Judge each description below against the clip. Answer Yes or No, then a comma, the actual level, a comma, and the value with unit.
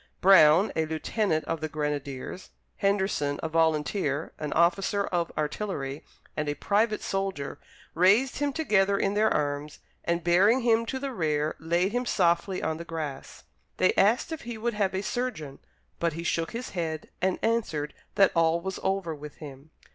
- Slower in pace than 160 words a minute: No, average, 170 wpm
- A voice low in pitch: No, medium, 170 Hz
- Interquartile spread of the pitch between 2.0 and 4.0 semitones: No, average, 4.8 semitones